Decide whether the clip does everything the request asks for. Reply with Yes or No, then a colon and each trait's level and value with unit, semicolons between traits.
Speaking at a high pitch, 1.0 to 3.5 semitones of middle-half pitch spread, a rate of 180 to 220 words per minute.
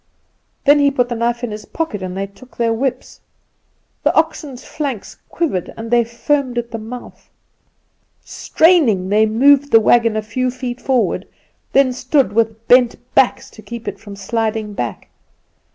No: high, 235 Hz; average, 3.2 semitones; average, 165 wpm